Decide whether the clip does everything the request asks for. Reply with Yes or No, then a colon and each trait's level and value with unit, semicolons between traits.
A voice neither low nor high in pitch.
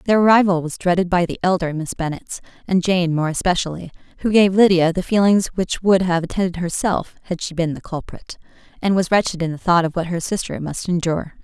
Yes: medium, 180 Hz